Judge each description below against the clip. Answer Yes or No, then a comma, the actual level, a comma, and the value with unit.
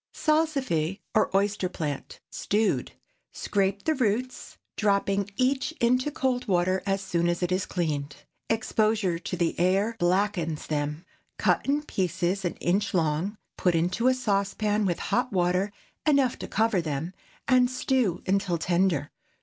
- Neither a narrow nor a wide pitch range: Yes, average, 4.5 semitones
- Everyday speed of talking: Yes, average, 145 wpm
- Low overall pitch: No, high, 195 Hz